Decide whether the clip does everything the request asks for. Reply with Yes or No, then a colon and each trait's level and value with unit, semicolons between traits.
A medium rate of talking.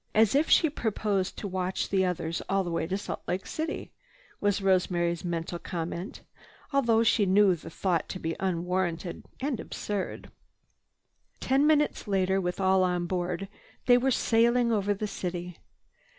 Yes: average, 160 wpm